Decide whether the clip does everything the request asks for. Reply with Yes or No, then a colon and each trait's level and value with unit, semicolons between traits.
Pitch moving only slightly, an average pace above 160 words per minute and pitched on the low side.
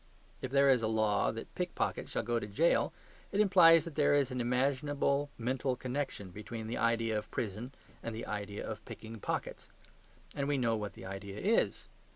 No: average, 4.4 semitones; average, 190 wpm; low, 120 Hz